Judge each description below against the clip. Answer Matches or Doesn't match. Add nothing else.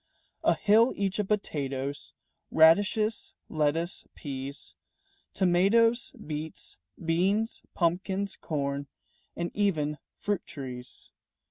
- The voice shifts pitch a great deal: Matches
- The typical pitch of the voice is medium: Matches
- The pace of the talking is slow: Matches